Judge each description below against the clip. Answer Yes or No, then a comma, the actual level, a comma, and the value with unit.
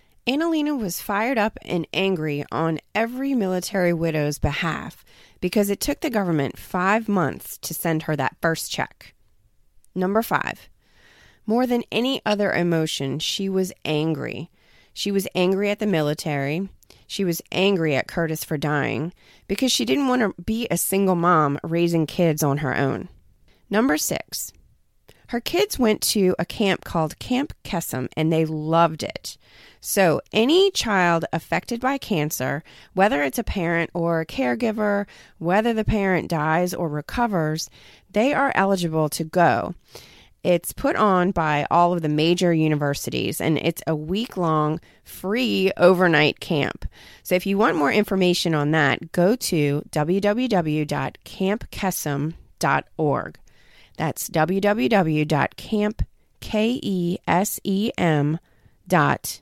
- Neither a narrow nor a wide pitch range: Yes, average, 4.7 semitones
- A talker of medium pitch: Yes, medium, 175 Hz